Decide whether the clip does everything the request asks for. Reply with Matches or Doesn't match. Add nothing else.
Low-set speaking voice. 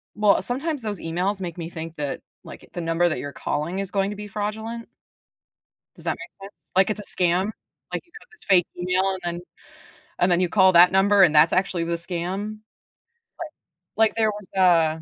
Doesn't match